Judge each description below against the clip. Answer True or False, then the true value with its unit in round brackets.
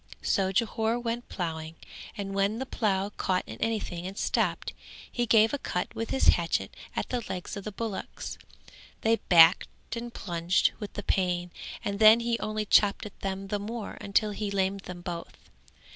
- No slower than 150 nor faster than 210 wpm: True (175 wpm)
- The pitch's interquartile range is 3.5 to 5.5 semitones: False (3.0 semitones)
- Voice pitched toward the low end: False (200 Hz)